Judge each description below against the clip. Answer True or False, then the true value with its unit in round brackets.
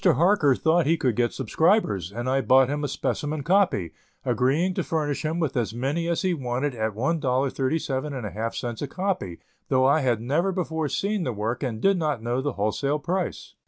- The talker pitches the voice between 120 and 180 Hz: True (140 Hz)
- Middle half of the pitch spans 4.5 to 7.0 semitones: True (5.2 semitones)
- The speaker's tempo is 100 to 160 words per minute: False (185 wpm)